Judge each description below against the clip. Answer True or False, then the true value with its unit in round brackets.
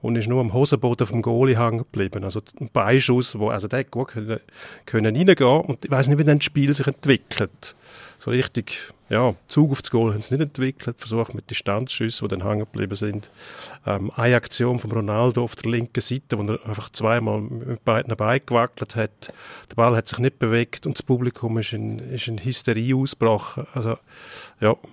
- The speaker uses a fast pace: True (195 wpm)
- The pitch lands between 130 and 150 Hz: False (120 Hz)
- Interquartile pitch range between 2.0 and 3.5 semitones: True (2.8 semitones)